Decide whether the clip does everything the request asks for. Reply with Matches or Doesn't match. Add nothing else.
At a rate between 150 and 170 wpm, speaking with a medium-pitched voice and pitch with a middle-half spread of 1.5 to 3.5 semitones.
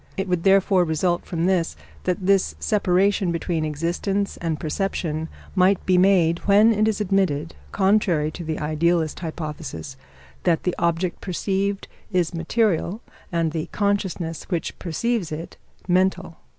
Doesn't match